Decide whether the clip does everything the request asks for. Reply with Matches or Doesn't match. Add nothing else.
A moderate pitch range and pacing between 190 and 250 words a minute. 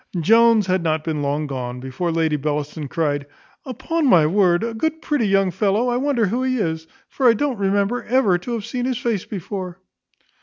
Doesn't match